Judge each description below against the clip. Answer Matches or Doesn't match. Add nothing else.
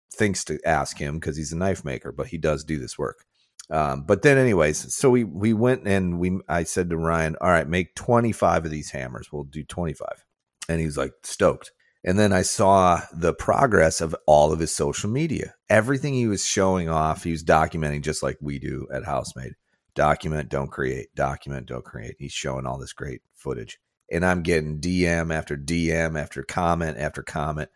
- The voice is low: Matches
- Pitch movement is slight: Doesn't match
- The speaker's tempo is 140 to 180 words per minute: Doesn't match